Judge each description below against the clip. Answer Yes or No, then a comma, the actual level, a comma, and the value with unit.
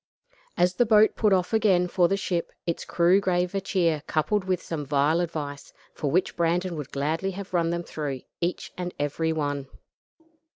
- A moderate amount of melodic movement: Yes, average, 3.2 semitones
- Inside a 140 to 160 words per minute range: No, average, 180 wpm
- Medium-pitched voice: Yes, medium, 175 Hz